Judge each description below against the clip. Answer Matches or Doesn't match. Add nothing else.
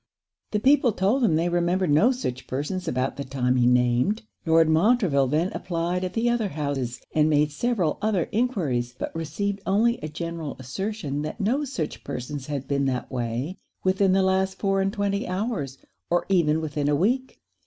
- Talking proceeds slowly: Doesn't match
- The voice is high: Doesn't match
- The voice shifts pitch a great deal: Matches